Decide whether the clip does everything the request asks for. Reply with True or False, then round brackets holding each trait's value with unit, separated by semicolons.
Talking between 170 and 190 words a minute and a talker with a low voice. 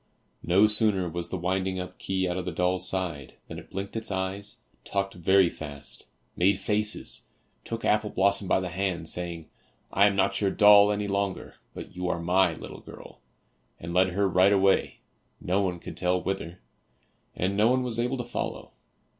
True (185 wpm; 95 Hz)